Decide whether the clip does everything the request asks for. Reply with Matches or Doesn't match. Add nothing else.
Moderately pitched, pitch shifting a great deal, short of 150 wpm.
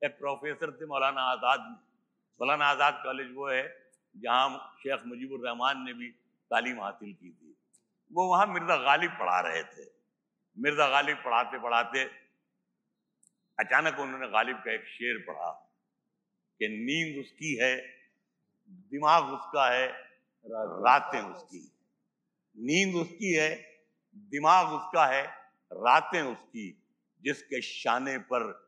Matches